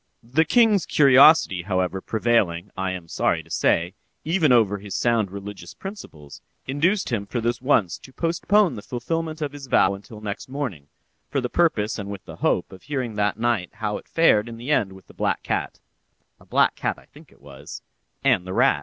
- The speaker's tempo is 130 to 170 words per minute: No, average, 200 wpm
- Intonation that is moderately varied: No, wide, 7.0 semitones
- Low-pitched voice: Yes, low, 115 Hz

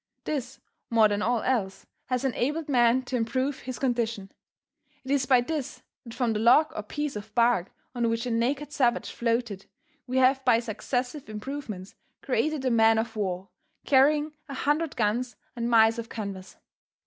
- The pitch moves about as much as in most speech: Yes, average, 3.1 semitones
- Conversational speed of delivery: Yes, average, 170 wpm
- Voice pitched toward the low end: No, high, 240 Hz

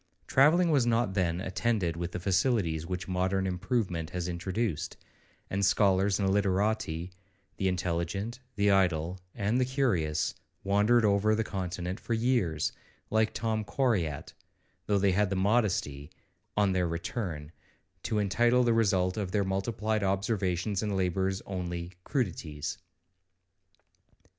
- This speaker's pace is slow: Yes, slow, 130 wpm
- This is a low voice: Yes, very low, 95 Hz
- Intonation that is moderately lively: Yes, average, 3.5 semitones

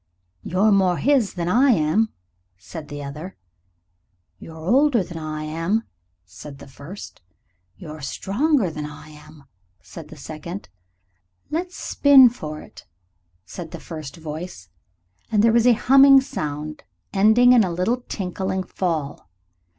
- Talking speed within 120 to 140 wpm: Yes, slow, 135 wpm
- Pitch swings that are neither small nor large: No, wide, 6.7 semitones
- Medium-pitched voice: Yes, medium, 180 Hz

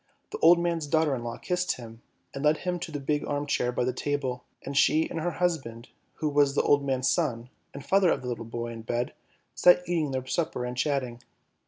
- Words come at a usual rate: No, fast, 225 wpm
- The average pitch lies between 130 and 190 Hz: Yes, medium, 140 Hz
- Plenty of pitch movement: No, average, 4.6 semitones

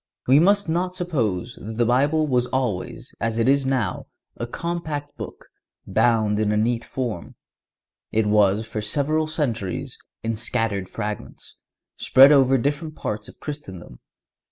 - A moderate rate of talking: Yes, average, 145 wpm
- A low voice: Yes, low, 120 Hz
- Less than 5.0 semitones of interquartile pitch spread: No, wide, 5.4 semitones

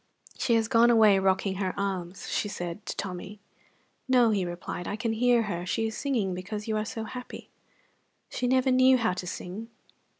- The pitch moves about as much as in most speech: Yes, average, 3.8 semitones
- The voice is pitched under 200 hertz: No, high, 215 Hz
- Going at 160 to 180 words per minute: No, average, 190 wpm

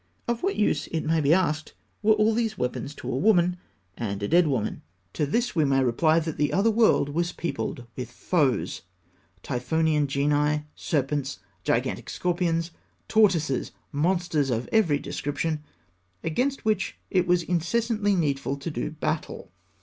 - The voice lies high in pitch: No, medium, 160 Hz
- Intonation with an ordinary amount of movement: Yes, average, 4.5 semitones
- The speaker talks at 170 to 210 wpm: No, average, 150 wpm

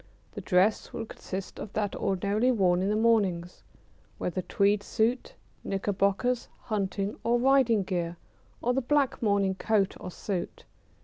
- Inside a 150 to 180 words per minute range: No, average, 140 wpm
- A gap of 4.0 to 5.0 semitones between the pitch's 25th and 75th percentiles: No, average, 3.3 semitones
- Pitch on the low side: No, high, 205 Hz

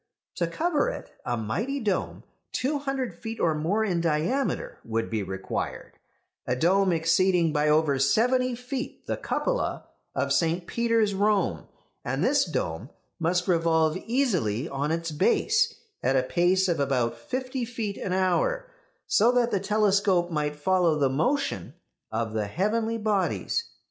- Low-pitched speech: No, medium, 180 Hz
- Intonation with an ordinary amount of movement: No, wide, 7.2 semitones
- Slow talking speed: No, average, 150 wpm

